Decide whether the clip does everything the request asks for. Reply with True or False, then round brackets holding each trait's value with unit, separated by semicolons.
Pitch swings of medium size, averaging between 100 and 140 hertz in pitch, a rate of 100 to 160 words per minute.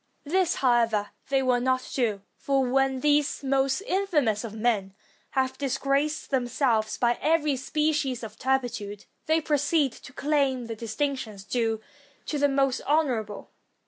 False (3.7 semitones; 265 Hz; 145 wpm)